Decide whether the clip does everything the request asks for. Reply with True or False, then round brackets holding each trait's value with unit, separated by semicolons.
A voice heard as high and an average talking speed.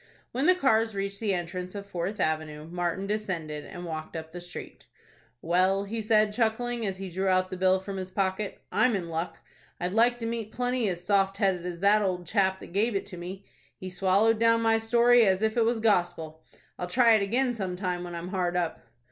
False (195 Hz; 215 wpm)